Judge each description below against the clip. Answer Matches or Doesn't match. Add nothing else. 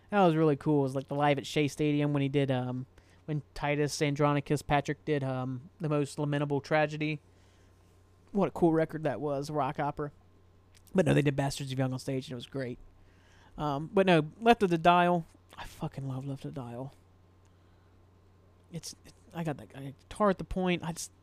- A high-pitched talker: Doesn't match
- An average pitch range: Doesn't match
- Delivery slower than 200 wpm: Doesn't match